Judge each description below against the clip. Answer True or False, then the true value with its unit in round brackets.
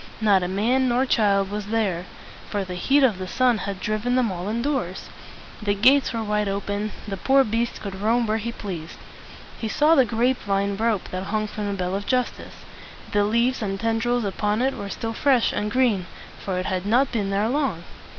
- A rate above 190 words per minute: True (205 wpm)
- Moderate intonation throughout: True (3.5 semitones)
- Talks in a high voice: True (215 Hz)